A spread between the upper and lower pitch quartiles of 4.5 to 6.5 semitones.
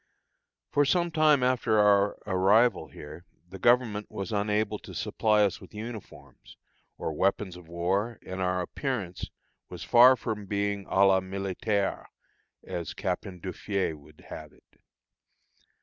No: average, 3.3 semitones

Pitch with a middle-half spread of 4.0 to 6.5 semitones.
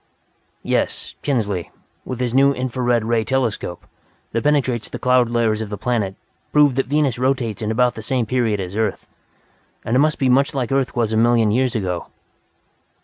No: average, 3.0 semitones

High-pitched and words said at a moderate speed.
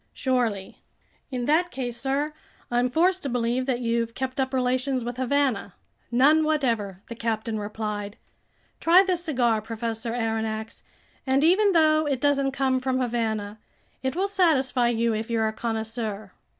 Yes: high, 245 Hz; average, 150 wpm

